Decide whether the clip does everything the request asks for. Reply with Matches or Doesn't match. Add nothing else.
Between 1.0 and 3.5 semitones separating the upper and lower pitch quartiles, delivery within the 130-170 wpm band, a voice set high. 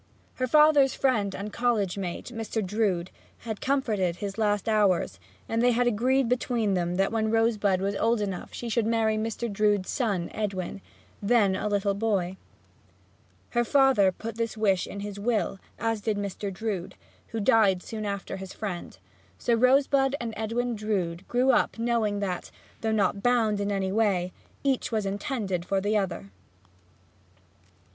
Matches